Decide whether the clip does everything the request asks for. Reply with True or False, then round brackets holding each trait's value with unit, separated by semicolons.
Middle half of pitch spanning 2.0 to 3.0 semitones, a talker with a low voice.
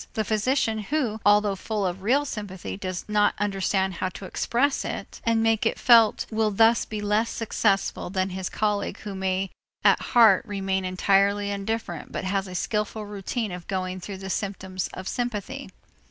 False (2.5 semitones; 205 Hz)